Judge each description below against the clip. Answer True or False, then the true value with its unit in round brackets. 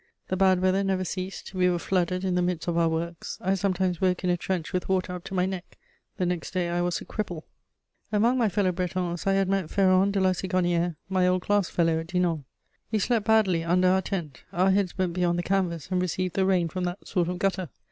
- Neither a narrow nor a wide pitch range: False (1.5 semitones)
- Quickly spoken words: True (240 wpm)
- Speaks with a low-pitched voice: False (185 Hz)